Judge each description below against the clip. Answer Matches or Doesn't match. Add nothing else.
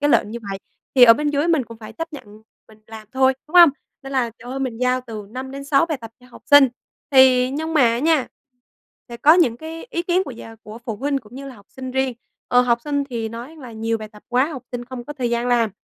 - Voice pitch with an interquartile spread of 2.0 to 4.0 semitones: Matches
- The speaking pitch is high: Matches